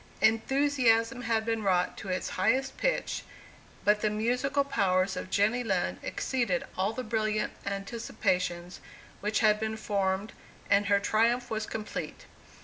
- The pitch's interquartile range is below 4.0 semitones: Yes, average, 3.0 semitones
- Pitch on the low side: No, high, 215 Hz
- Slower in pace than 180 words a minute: Yes, average, 140 wpm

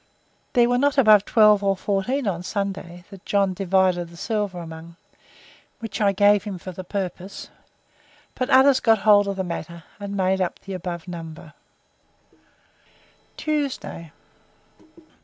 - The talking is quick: No, average, 145 wpm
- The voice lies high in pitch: Yes, high, 195 Hz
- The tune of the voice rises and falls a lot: No, average, 3.1 semitones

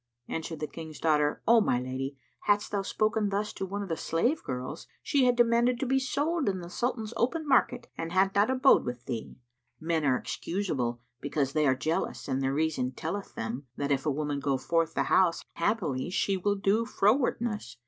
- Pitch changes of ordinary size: No, wide, 7.6 semitones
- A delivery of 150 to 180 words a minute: No, average, 200 wpm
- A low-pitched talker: No, medium, 170 Hz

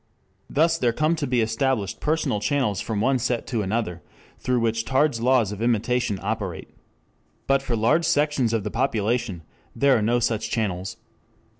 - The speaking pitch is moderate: No, low, 120 Hz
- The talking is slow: No, average, 165 wpm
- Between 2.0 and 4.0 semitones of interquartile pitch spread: Yes, average, 3.7 semitones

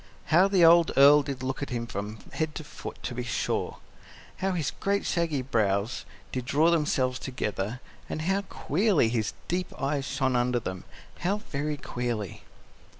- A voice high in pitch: No, medium, 140 Hz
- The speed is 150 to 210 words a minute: Yes, average, 165 wpm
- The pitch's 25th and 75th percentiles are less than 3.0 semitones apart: No, average, 5.2 semitones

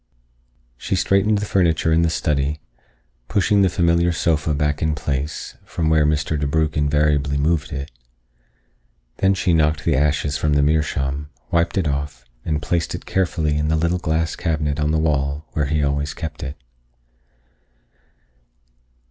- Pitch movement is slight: Yes, narrow, 2.1 semitones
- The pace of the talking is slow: No, average, 155 wpm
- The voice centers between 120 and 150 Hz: No, very low, 75 Hz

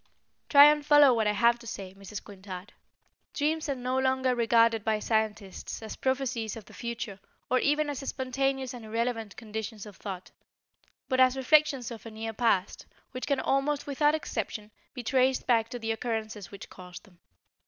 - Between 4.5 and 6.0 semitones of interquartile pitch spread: No, average, 3.5 semitones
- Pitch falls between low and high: No, high, 235 Hz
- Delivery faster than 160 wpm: Yes, average, 175 wpm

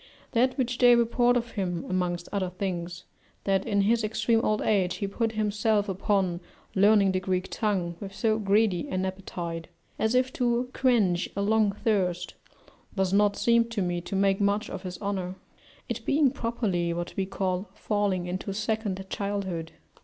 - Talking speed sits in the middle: Yes, average, 170 wpm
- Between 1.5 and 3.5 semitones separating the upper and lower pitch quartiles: Yes, average, 3.2 semitones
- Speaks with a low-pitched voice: No, high, 200 Hz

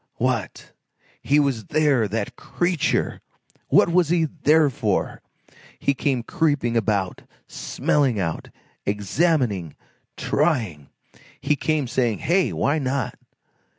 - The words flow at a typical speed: No, slow, 110 wpm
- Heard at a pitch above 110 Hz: Yes, low, 135 Hz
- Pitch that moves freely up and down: Yes, wide, 6.0 semitones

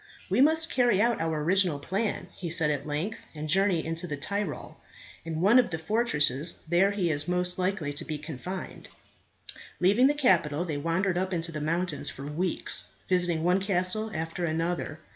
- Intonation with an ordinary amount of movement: Yes, average, 3.7 semitones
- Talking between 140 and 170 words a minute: No, average, 180 wpm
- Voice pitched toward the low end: No, medium, 175 Hz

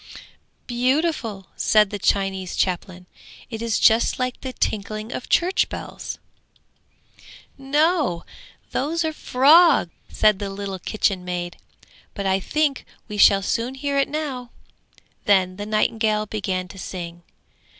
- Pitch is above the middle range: Yes, high, 215 Hz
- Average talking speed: No, slow, 130 wpm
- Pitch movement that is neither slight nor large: No, wide, 5.7 semitones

